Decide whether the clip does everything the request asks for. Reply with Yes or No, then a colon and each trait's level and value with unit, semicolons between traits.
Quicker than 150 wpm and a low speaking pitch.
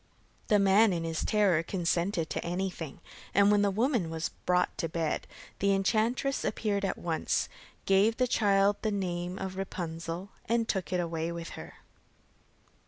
No: average, 160 wpm; high, 190 Hz